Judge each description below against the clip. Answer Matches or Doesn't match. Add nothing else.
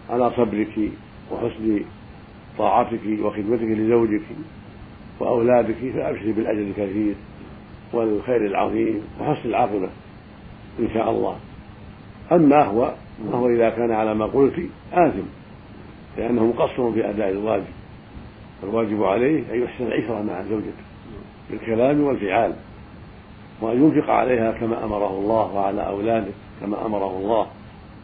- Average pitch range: Doesn't match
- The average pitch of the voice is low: Matches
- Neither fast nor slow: Matches